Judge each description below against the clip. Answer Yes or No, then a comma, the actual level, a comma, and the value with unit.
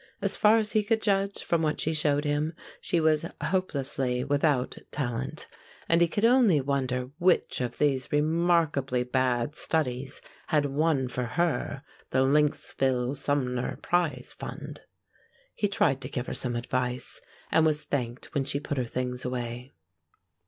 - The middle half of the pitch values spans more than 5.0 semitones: No, average, 4.0 semitones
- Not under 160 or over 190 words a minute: No, average, 150 wpm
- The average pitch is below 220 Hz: Yes, medium, 140 Hz